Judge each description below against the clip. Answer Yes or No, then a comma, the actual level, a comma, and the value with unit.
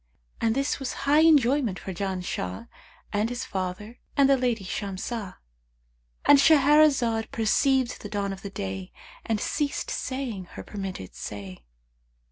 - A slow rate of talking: Yes, slow, 125 wpm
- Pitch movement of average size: No, wide, 6.6 semitones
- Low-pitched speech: No, high, 215 Hz